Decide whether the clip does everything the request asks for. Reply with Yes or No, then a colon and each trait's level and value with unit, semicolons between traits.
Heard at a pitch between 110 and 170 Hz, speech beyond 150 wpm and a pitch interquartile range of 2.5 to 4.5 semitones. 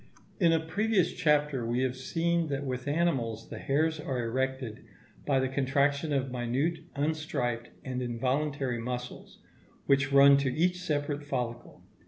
No: medium, 140 Hz; average, 145 wpm; average, 3.3 semitones